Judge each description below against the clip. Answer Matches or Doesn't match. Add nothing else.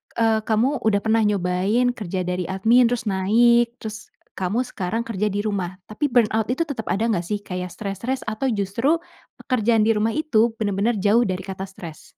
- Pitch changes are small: Doesn't match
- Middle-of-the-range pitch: Doesn't match